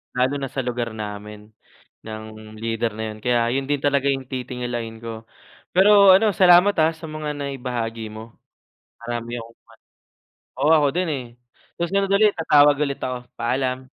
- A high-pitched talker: No, low, 130 Hz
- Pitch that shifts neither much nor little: Yes, average, 4.5 semitones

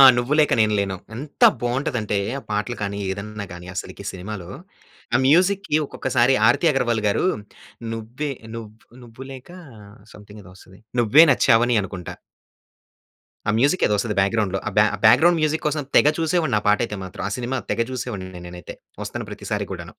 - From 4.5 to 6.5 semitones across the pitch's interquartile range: Yes, average, 4.8 semitones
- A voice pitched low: Yes, low, 115 Hz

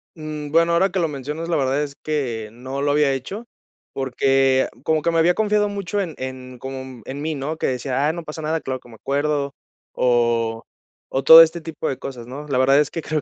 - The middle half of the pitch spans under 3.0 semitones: No, average, 3.5 semitones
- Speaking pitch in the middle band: Yes, medium, 145 Hz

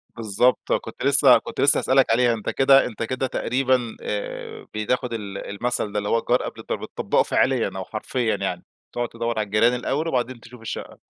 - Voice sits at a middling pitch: No, low, 120 Hz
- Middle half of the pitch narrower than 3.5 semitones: Yes, narrow, 2.6 semitones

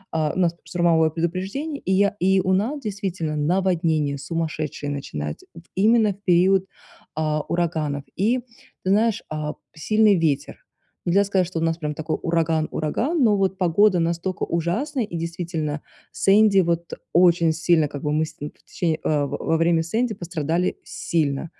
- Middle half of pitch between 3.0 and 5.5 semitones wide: Yes, average, 3.5 semitones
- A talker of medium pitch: Yes, medium, 170 Hz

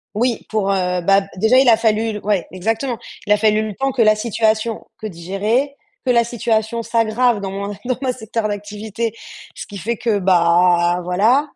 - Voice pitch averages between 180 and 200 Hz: No, high, 215 Hz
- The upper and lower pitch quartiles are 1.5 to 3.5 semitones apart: Yes, average, 2.9 semitones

